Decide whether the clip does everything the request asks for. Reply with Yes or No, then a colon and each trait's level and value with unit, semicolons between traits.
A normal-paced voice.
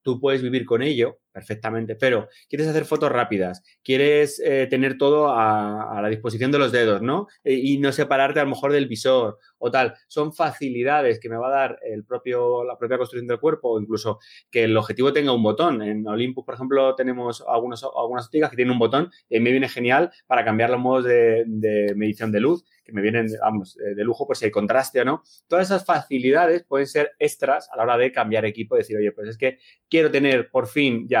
No: fast, 225 wpm